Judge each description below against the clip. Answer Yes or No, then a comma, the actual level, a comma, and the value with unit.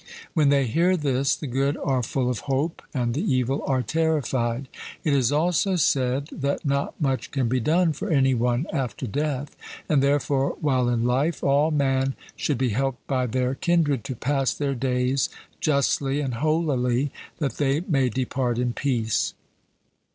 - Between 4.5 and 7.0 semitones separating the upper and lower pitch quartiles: No, narrow, 2.6 semitones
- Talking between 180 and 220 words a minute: No, average, 165 wpm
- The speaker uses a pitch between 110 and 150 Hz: Yes, low, 135 Hz